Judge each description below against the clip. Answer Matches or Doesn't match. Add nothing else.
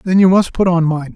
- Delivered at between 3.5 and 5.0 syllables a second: Doesn't match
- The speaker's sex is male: Matches